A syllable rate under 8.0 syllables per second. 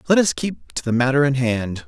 Yes: 5.3 syllables/s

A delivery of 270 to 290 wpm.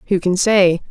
No: average, 200 wpm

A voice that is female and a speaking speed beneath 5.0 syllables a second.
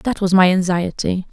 Yes: female; 4.8 syllables/s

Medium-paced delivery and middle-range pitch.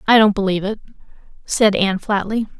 No: average, 160 wpm; high, 205 Hz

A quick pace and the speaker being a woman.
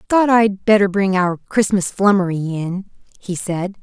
No: average, 155 wpm; female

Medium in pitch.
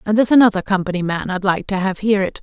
No: high, 200 Hz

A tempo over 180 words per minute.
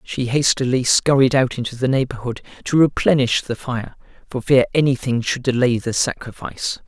No: average, 155 wpm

